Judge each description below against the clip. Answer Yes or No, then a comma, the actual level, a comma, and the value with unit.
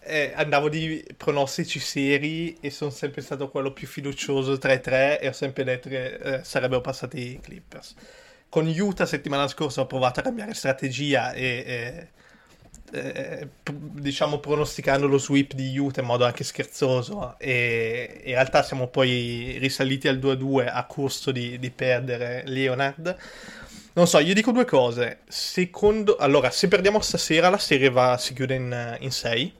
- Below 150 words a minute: No, average, 160 wpm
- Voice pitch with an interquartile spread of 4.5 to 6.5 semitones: No, average, 2.9 semitones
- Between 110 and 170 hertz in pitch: Yes, medium, 140 Hz